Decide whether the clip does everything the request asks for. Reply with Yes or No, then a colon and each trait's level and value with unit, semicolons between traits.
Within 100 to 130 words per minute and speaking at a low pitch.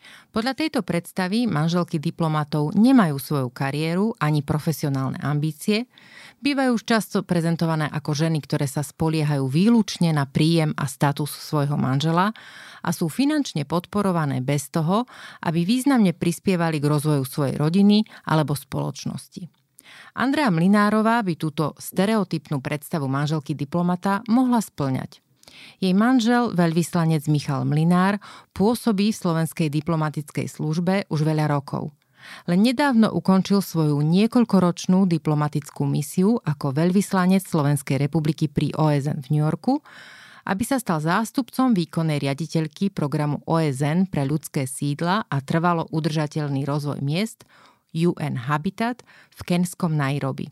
No: average, 120 wpm; medium, 165 Hz